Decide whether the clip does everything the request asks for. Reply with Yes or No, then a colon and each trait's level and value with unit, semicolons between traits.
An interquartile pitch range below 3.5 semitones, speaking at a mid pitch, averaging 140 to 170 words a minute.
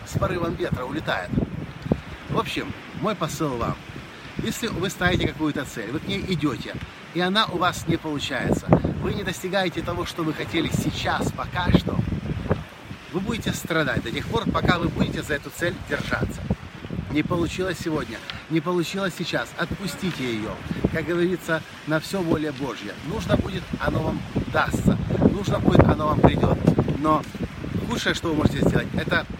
Yes: average, 2.9 semitones; medium, 165 Hz; fast, 160 wpm